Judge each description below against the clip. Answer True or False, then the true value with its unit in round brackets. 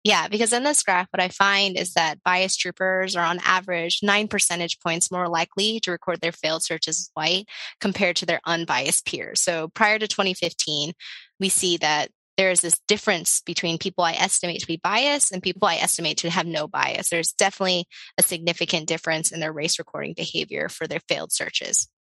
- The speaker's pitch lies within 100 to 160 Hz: False (175 Hz)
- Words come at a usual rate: True (195 wpm)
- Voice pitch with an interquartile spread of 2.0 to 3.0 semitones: True (2.4 semitones)